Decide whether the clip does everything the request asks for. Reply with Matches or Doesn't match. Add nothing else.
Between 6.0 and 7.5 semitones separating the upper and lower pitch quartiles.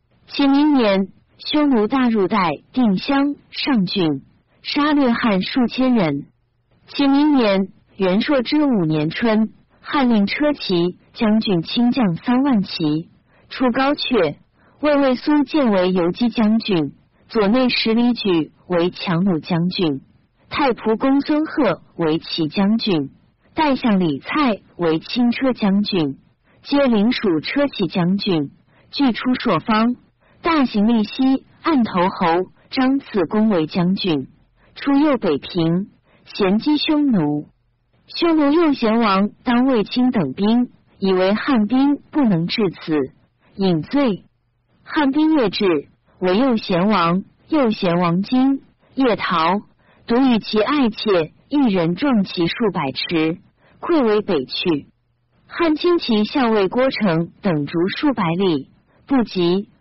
Matches